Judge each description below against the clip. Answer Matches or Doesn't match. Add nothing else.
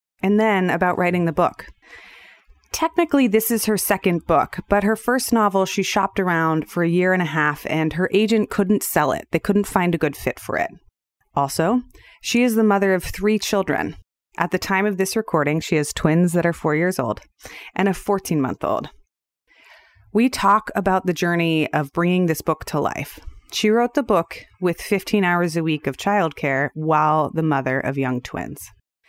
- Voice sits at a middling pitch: Matches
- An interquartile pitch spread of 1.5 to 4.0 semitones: Doesn't match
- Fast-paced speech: Doesn't match